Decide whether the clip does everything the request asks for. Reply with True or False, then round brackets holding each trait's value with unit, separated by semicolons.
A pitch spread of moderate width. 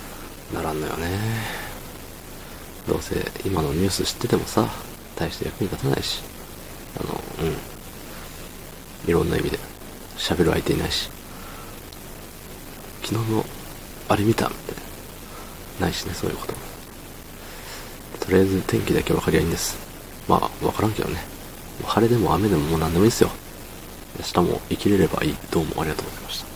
True (4.6 semitones)